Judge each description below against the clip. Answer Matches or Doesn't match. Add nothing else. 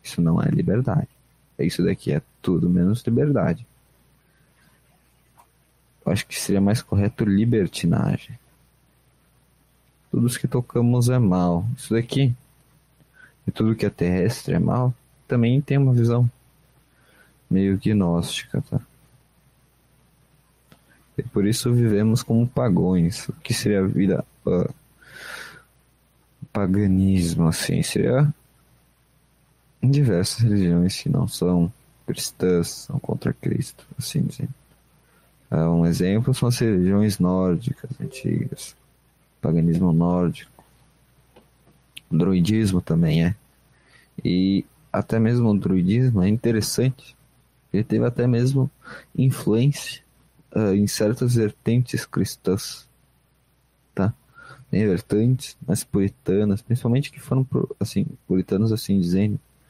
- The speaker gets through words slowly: Matches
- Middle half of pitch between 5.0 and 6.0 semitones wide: Matches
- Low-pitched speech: Matches